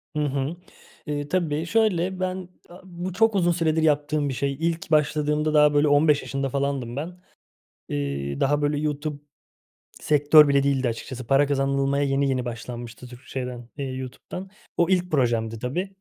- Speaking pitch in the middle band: Yes, medium, 145 Hz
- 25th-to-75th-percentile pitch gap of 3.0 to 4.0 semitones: Yes, average, 3.4 semitones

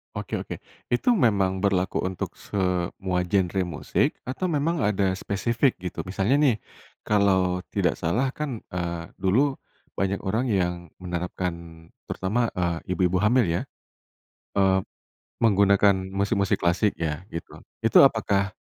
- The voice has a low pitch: Yes, very low, 95 Hz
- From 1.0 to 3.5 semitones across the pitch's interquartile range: Yes, average, 2.7 semitones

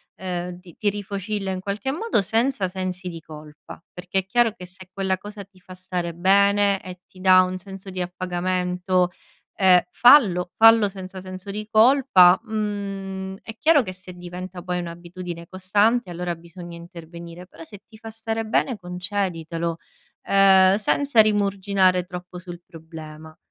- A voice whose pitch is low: No, medium, 185 Hz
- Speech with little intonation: Yes, narrow, 2.3 semitones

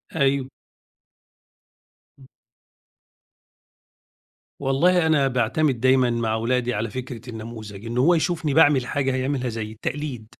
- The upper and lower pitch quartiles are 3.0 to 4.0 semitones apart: Yes, average, 3.5 semitones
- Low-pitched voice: Yes, low, 130 Hz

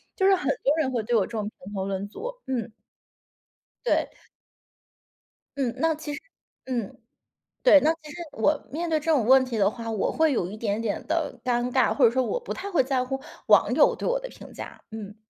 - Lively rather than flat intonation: Yes, wide, 5.7 semitones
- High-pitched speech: Yes, very high, 260 Hz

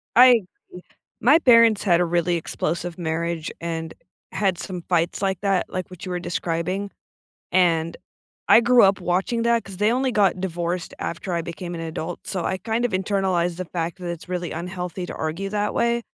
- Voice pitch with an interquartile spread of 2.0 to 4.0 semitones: Yes, average, 2.8 semitones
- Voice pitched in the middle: Yes, medium, 180 Hz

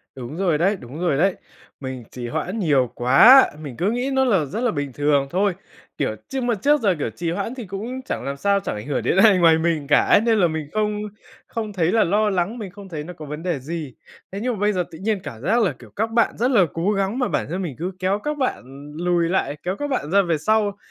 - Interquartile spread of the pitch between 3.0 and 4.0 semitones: No, wide, 5.6 semitones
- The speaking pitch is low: No, medium, 185 Hz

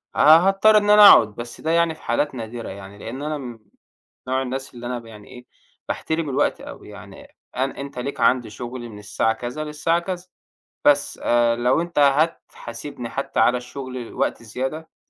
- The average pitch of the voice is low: Yes, low, 130 Hz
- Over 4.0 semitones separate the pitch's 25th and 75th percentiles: Yes, average, 4.4 semitones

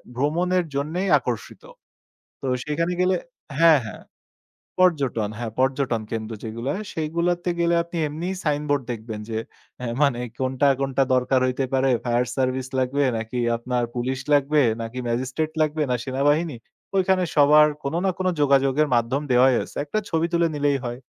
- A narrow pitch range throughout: No, average, 4.0 semitones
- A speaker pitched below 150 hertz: Yes, medium, 140 Hz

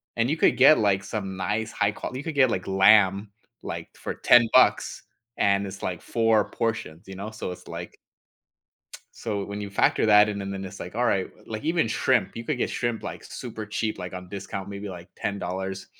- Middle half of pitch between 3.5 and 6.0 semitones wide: No, average, 2.7 semitones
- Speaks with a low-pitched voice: Yes, low, 100 Hz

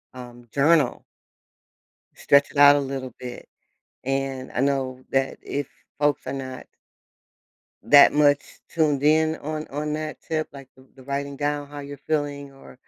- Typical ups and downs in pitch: No, narrow, 1.6 semitones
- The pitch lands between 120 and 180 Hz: Yes, medium, 140 Hz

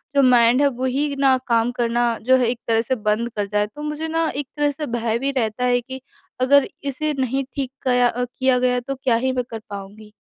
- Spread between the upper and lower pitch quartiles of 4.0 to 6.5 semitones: No, average, 2.8 semitones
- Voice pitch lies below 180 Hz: No, very high, 250 Hz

